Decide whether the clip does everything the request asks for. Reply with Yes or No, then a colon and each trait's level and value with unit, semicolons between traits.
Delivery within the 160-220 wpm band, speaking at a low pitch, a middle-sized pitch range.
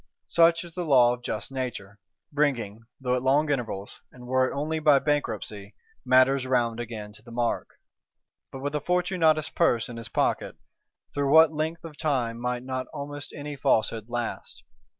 Yes: average, 170 wpm; low, 130 Hz; average, 3.9 semitones